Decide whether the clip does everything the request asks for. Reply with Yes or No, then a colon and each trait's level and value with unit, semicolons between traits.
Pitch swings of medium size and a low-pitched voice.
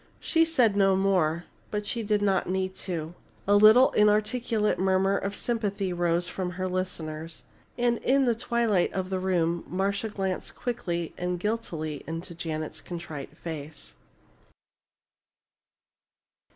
No: average, 3.5 semitones; high, 190 Hz